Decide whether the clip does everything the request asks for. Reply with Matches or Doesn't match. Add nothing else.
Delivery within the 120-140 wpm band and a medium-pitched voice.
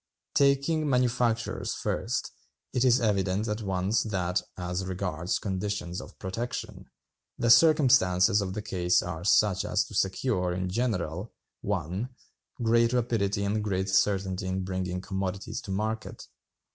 Doesn't match